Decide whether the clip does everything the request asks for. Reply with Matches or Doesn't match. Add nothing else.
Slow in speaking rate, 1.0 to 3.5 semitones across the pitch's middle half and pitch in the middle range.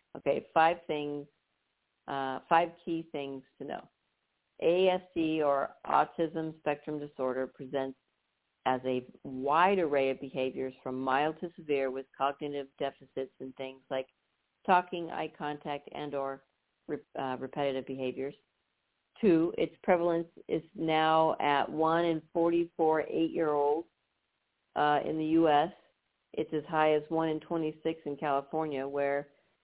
Matches